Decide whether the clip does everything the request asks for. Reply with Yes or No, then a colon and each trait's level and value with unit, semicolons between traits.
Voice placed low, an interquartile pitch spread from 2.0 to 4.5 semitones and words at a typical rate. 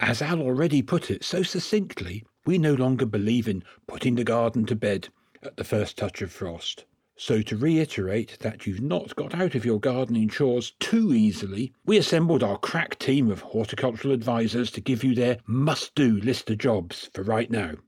No: low, 125 Hz; average, 5.0 semitones; average, 190 wpm